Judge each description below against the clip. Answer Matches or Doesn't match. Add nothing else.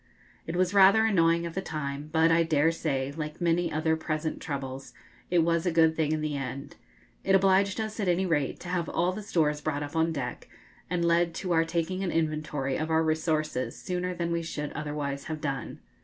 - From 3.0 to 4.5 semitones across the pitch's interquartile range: Doesn't match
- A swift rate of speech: Matches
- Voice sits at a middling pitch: Matches